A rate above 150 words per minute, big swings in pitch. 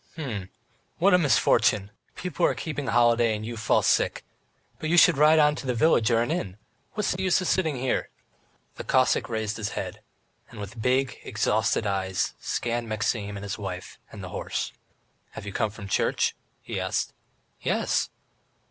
Yes: average, 175 wpm; wide, 5.9 semitones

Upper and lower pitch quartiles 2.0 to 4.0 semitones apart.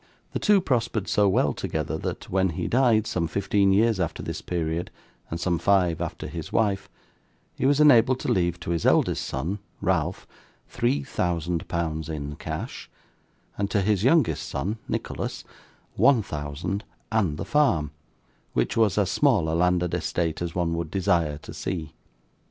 No: average, 4.5 semitones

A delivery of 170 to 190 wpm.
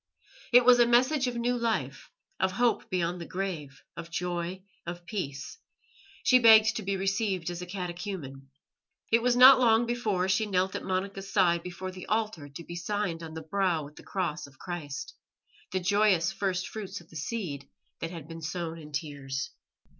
Yes: average, 185 wpm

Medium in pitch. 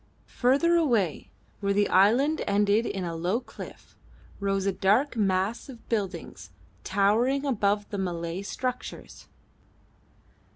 No: high, 205 Hz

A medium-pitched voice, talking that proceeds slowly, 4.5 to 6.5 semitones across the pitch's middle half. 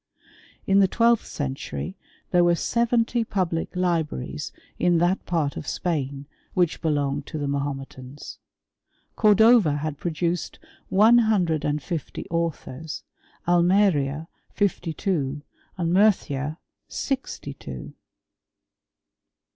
Yes: medium, 170 Hz; slow, 105 wpm; average, 5.1 semitones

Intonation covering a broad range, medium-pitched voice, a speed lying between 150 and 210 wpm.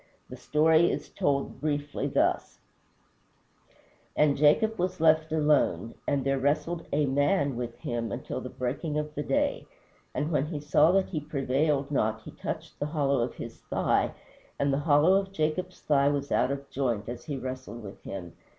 No: narrow, 2.6 semitones; medium, 145 Hz; average, 170 wpm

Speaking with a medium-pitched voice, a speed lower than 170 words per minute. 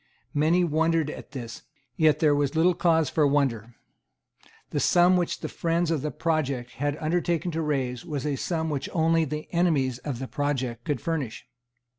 No: medium, 150 Hz; average, 175 wpm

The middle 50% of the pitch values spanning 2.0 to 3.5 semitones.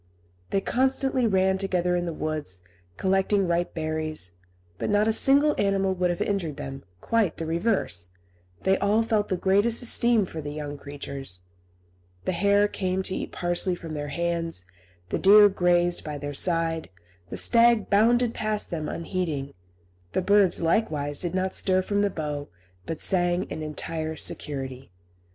No: average, 4.5 semitones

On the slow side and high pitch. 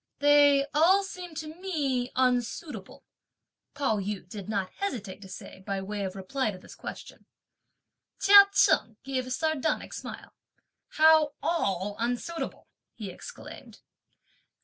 Yes: slow, 125 wpm; very high, 260 Hz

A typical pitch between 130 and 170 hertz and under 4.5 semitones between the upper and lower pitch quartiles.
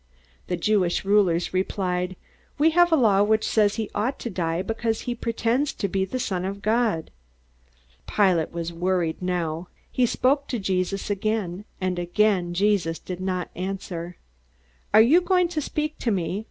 No: high, 195 Hz; average, 4.1 semitones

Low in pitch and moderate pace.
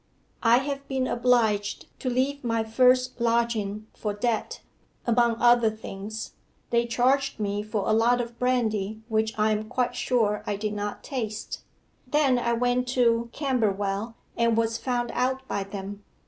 No: high, 230 Hz; average, 155 wpm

